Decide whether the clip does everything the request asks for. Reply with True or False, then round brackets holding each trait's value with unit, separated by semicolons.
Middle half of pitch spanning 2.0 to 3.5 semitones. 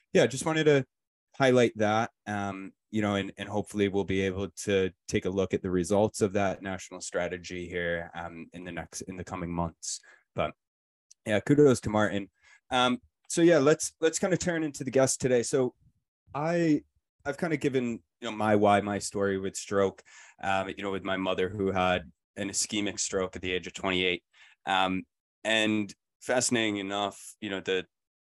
False (4.4 semitones)